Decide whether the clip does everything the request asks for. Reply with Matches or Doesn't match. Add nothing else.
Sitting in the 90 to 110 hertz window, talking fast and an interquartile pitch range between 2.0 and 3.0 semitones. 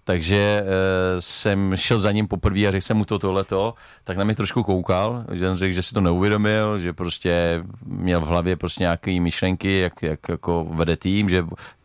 Matches